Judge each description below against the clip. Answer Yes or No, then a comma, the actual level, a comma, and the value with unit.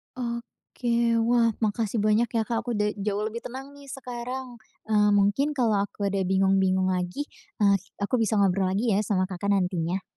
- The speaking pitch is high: Yes, high, 210 Hz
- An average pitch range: Yes, average, 3.3 semitones